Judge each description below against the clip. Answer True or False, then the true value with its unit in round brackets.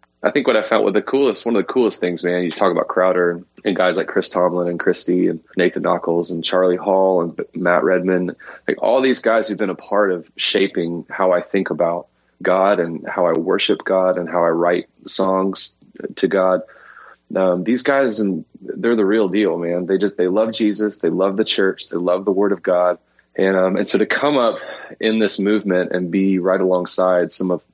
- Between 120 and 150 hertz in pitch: False (90 Hz)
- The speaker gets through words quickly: True (220 wpm)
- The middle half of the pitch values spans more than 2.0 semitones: False (1.5 semitones)